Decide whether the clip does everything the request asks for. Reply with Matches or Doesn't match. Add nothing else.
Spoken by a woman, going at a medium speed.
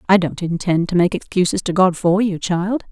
Doesn't match